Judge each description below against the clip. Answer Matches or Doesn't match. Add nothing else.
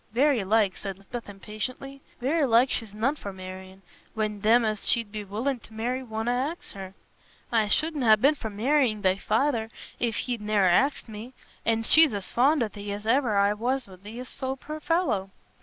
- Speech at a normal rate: Matches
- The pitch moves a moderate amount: Matches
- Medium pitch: Doesn't match